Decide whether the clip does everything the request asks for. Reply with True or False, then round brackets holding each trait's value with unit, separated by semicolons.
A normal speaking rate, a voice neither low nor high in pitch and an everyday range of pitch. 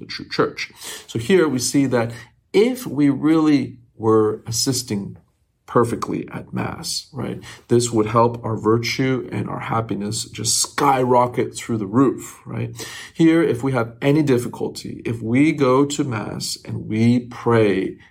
False (150 wpm; 120 Hz; 3.2 semitones)